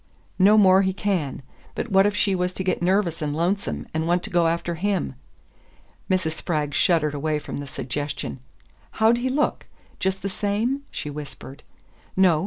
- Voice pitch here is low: No, medium, 180 Hz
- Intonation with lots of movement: No, average, 4.4 semitones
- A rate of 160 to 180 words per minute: Yes, average, 175 wpm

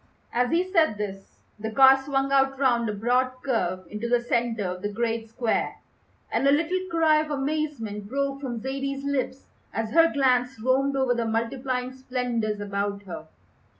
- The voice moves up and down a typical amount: Yes, average, 3.6 semitones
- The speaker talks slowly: No, average, 170 wpm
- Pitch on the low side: No, very high, 250 Hz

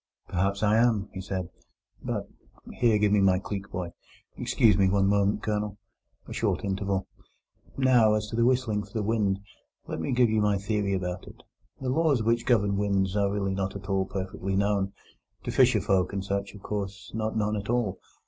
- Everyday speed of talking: Yes, average, 175 wpm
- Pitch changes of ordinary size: No, narrow, 1.9 semitones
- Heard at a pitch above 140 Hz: No, low, 100 Hz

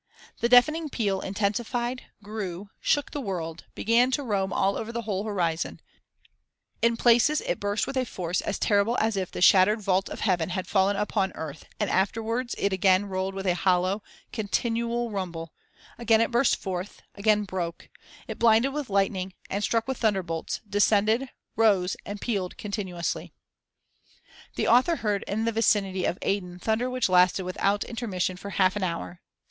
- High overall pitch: Yes, high, 205 Hz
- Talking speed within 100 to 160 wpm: No, average, 170 wpm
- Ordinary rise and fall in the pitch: Yes, average, 3.5 semitones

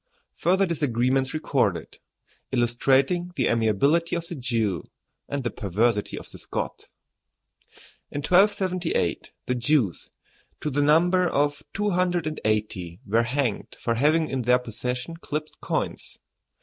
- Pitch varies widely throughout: Yes, wide, 5.9 semitones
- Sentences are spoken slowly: Yes, slow, 130 wpm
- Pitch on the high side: No, low, 135 Hz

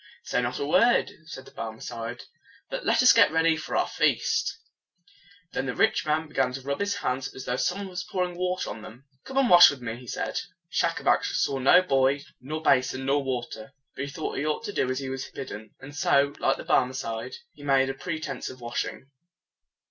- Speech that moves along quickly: Yes, fast, 215 wpm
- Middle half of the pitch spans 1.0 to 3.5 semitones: No, average, 4.2 semitones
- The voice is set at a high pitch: No, low, 135 Hz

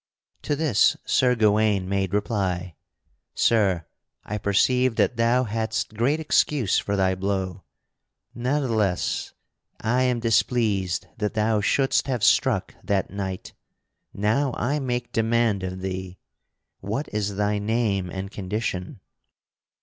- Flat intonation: No, average, 3.7 semitones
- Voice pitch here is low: Yes, low, 105 Hz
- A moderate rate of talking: No, slow, 120 wpm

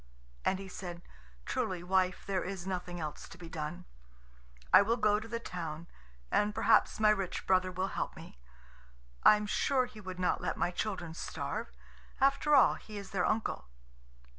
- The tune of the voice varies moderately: Yes, average, 3.1 semitones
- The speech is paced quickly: No, average, 175 wpm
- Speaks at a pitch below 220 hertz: Yes, high, 190 Hz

